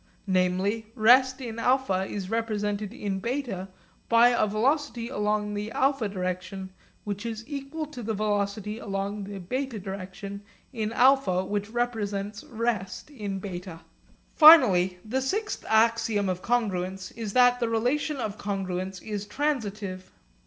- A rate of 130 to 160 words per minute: Yes, slow, 135 wpm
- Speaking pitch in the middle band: No, high, 210 Hz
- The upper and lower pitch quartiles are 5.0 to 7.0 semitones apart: No, average, 3.8 semitones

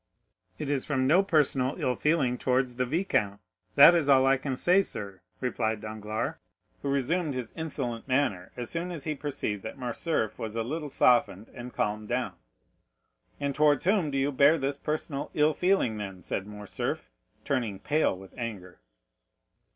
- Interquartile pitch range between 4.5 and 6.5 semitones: Yes, average, 5.3 semitones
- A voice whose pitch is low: Yes, low, 130 Hz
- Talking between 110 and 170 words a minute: Yes, average, 165 wpm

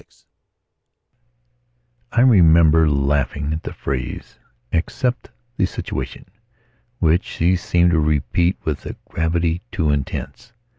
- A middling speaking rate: No, slow, 110 wpm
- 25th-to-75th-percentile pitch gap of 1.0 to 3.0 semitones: Yes, average, 2.7 semitones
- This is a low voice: Yes, very low, 80 Hz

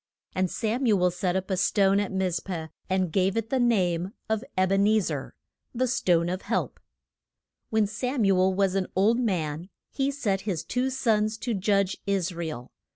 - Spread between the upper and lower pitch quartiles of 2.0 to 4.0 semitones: Yes, average, 3.3 semitones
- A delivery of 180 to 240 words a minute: Yes, average, 200 wpm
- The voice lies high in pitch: Yes, high, 195 Hz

